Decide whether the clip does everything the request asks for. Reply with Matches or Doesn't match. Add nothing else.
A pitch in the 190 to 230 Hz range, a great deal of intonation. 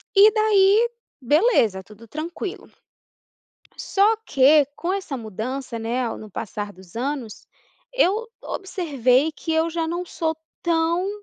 Doesn't match